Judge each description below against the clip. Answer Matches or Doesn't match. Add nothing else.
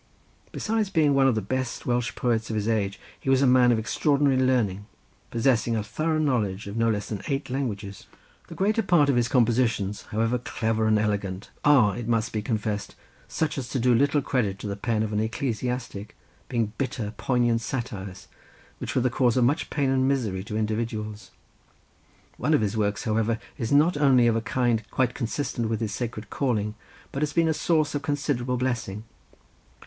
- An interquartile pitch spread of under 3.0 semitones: Doesn't match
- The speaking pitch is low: Matches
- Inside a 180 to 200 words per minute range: Matches